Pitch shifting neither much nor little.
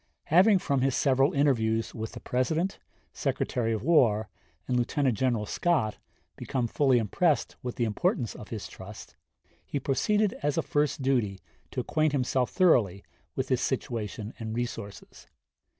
Yes: average, 4.6 semitones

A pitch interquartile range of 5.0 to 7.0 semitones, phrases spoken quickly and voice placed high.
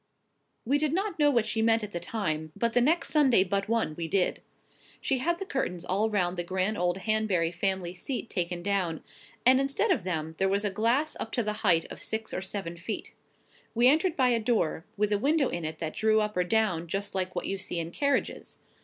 Yes: wide, 5.5 semitones; fast, 225 wpm; high, 210 Hz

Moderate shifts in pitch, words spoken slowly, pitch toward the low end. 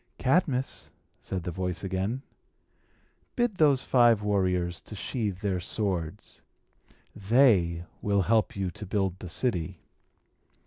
Yes: average, 4.6 semitones; slow, 120 wpm; low, 100 Hz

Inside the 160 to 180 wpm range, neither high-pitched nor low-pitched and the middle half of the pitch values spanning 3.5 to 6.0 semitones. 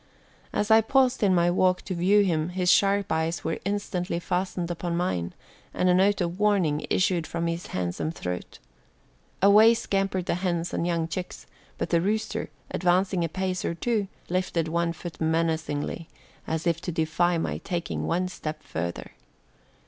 No: average, 165 wpm; medium, 175 Hz; narrow, 2.4 semitones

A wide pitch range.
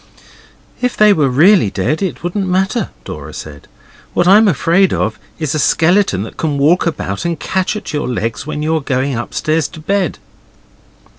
Yes: wide, 6.0 semitones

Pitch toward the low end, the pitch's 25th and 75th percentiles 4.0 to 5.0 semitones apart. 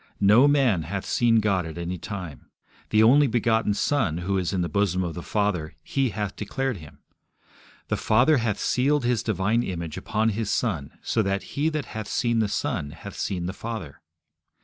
Yes: low, 105 Hz; average, 4.5 semitones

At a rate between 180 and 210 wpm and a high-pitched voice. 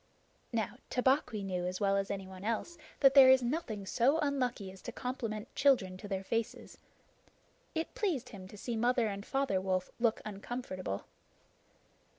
No: average, 160 wpm; high, 220 Hz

